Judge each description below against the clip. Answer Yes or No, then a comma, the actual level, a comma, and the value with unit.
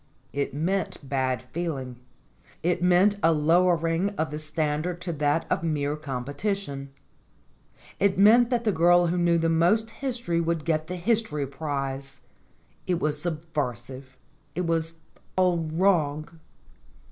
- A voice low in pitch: No, medium, 165 Hz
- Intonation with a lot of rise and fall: No, average, 3.5 semitones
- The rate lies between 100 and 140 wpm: Yes, slow, 135 wpm